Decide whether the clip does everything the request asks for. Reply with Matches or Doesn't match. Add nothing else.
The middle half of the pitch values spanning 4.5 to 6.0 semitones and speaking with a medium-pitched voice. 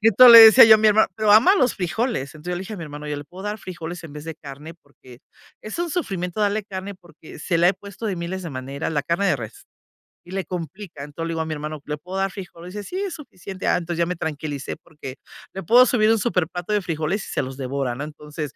Matches